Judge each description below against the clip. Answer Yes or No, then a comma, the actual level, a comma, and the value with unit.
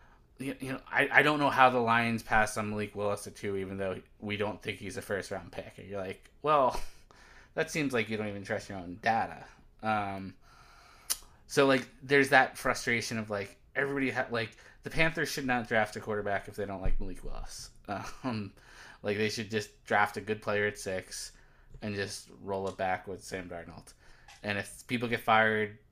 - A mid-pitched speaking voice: No, low, 105 Hz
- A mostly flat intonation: No, average, 3.1 semitones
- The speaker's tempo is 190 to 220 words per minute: Yes, average, 200 wpm